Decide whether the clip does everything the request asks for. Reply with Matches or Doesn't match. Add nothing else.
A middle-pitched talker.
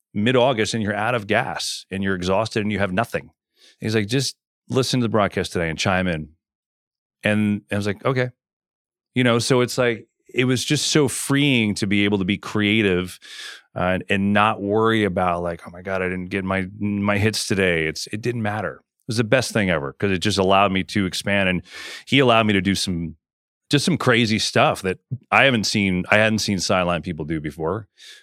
Doesn't match